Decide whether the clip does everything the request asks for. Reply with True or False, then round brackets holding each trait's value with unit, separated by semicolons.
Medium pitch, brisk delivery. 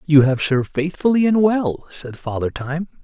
False (155 Hz; 180 wpm)